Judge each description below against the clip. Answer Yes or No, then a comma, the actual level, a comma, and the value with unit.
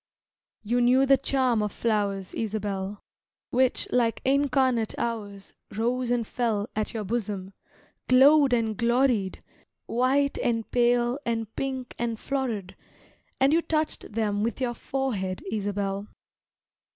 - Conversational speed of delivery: No, slow, 125 wpm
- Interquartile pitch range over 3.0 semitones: Yes, average, 3.6 semitones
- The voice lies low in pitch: No, high, 235 Hz